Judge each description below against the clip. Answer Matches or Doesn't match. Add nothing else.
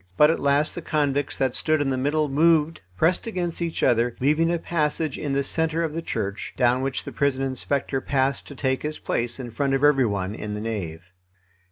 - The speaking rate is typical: Doesn't match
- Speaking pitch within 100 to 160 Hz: Matches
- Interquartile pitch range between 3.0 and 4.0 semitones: Matches